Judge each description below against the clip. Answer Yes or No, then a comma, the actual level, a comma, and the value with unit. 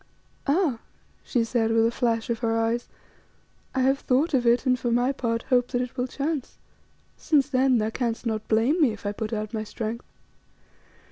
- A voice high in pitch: Yes, high, 240 Hz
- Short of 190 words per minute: No, average, 195 wpm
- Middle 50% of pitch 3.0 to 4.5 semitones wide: No, narrow, 2.5 semitones